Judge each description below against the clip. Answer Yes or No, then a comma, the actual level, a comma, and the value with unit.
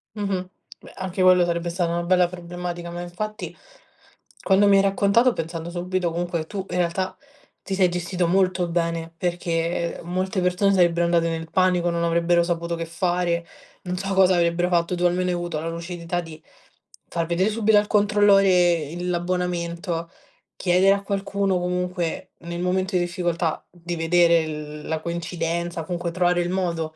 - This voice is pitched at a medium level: Yes, medium, 175 Hz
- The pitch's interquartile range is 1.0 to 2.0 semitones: Yes, narrow, 1.4 semitones